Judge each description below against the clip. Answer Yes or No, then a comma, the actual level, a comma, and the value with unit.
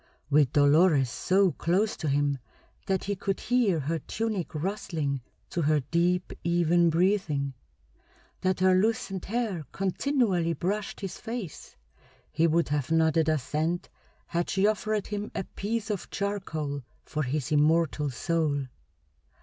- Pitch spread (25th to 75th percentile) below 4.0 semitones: No, average, 4.5 semitones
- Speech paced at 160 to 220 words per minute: No, slow, 135 wpm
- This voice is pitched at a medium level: Yes, medium, 170 Hz